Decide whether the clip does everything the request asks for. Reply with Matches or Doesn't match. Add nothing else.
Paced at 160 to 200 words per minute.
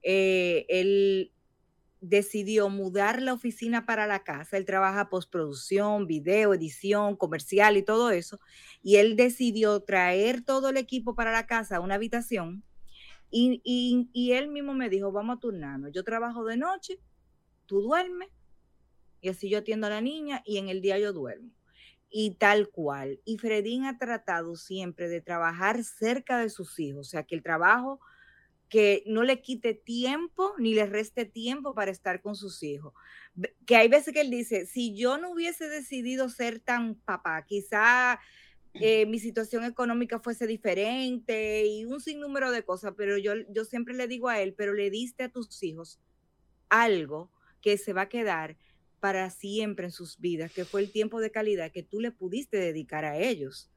Matches